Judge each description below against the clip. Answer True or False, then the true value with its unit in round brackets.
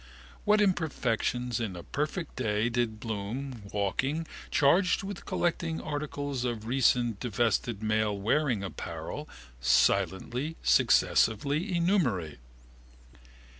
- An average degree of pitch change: False (5.9 semitones)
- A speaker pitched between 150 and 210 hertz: False (125 Hz)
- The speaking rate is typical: False (95 wpm)